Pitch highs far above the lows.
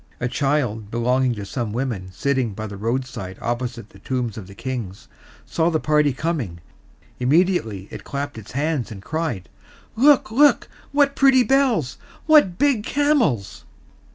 Yes: wide, 7.5 semitones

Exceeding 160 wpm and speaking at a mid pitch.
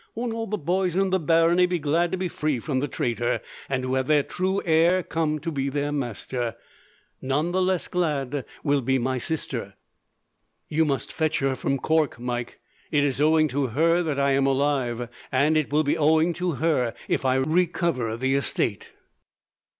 Yes: average, 190 wpm; medium, 145 Hz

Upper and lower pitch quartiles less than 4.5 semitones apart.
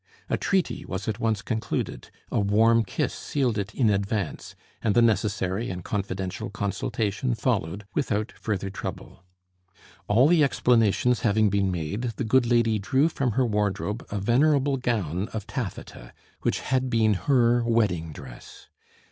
Yes: average, 3.4 semitones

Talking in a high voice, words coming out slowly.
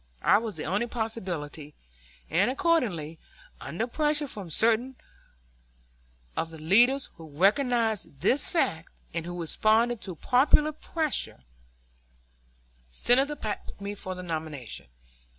Yes: high, 210 Hz; slow, 120 wpm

